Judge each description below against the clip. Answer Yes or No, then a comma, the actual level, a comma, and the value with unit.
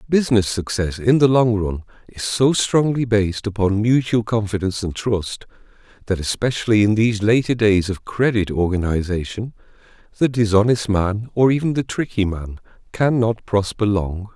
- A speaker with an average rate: Yes, average, 145 wpm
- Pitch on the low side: Yes, low, 105 Hz